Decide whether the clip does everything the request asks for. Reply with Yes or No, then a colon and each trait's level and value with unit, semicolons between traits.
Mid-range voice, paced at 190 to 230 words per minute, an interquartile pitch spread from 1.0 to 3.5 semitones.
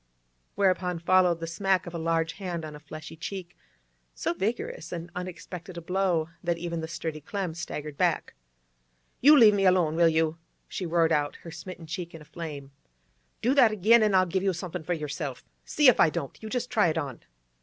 Yes: medium, 170 Hz; average, 200 wpm; average, 2.8 semitones